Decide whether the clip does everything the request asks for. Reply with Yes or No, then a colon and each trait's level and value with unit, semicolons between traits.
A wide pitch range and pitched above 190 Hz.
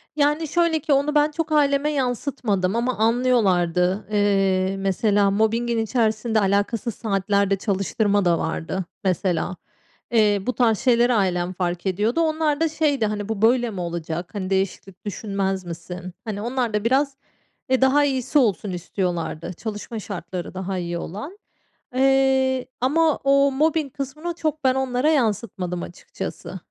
Yes: wide, 5.9 semitones; high, 220 Hz